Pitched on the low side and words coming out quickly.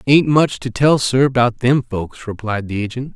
Yes: low, 125 Hz; fast, 210 wpm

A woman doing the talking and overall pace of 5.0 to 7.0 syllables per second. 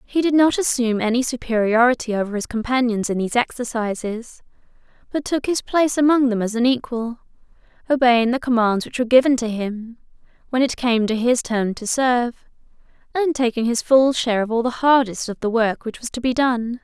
Yes: female; 5.6 syllables/s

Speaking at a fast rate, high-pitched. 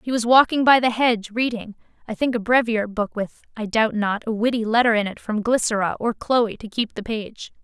Yes: fast, 230 wpm; high, 225 Hz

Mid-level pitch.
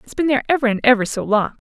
No: high, 240 Hz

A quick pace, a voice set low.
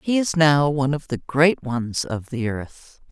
No: fast, 210 wpm; medium, 145 Hz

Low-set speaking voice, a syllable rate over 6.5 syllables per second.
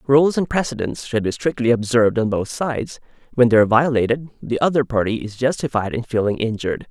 No: low, 120 Hz; 6.0 syllables/s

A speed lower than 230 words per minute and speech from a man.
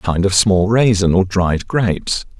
Yes: average, 200 wpm; male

